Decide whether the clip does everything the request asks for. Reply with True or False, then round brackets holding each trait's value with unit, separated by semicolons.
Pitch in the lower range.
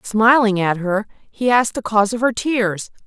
False (220 Hz)